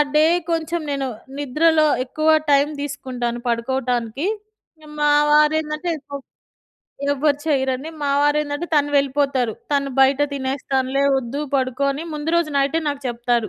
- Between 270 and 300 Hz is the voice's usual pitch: Yes, very high, 280 Hz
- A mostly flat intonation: Yes, narrow, 2.3 semitones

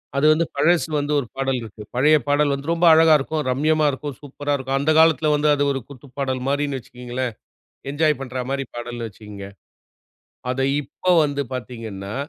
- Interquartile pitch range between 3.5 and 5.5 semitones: No, average, 3.0 semitones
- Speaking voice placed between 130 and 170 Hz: Yes, medium, 140 Hz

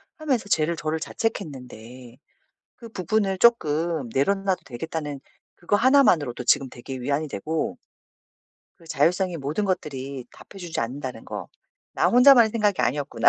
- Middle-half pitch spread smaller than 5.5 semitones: No, wide, 6.9 semitones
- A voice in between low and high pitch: Yes, medium, 160 Hz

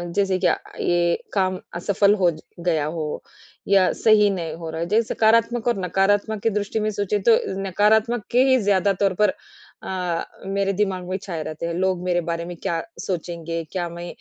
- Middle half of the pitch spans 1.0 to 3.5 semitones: Yes, average, 3.2 semitones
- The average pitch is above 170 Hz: Yes, high, 190 Hz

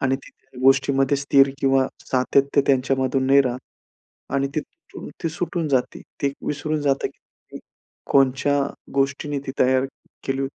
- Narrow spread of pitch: Yes, narrow, 1.0 semitones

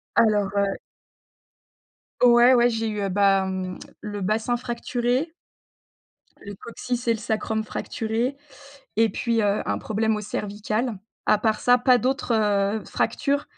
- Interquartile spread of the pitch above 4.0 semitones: No, average, 2.9 semitones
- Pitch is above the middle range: Yes, high, 220 Hz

